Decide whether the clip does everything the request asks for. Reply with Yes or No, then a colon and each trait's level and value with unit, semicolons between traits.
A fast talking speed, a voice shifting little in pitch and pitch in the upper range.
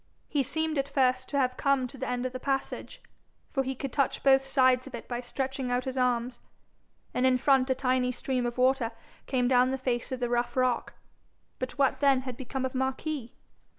Yes: fast, 215 wpm; narrow, 1.3 semitones; very high, 255 Hz